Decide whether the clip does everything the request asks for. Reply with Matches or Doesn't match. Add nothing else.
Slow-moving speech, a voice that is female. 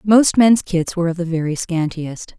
Doesn't match